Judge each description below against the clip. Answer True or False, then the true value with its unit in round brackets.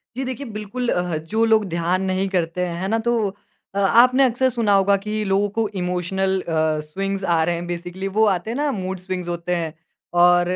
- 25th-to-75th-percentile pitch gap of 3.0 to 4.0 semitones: True (3.6 semitones)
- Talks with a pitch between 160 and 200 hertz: True (190 Hz)